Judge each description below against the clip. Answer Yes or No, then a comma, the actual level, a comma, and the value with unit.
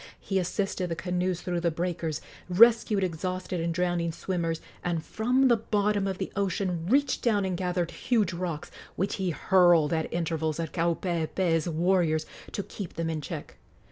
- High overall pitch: No, medium, 180 Hz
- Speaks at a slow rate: No, average, 165 wpm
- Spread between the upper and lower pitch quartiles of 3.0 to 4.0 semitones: No, narrow, 2.6 semitones